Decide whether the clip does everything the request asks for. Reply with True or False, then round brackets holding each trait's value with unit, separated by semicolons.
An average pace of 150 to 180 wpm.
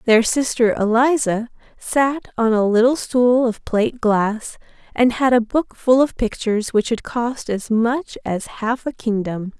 True (170 wpm)